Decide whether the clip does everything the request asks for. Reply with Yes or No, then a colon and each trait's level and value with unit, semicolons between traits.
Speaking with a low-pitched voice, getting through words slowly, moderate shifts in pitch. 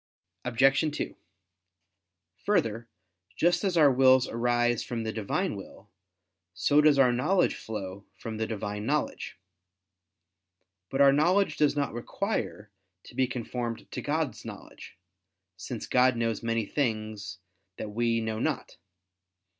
Yes: low, 120 Hz; slow, 130 wpm; average, 4.2 semitones